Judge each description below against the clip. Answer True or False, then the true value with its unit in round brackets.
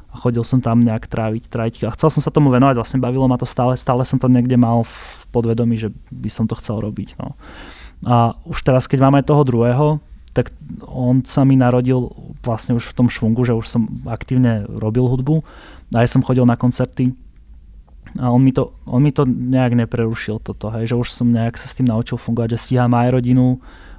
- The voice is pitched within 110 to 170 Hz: True (120 Hz)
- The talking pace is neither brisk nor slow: False (210 wpm)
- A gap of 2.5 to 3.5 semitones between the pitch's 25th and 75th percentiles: False (2.0 semitones)